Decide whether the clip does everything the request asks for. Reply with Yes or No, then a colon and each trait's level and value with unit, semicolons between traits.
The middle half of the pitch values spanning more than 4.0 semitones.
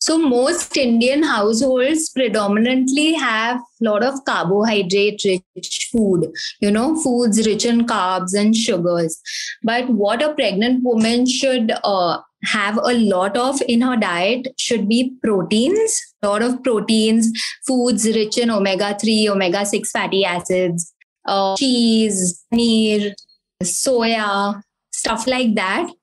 No: average, 3.7 semitones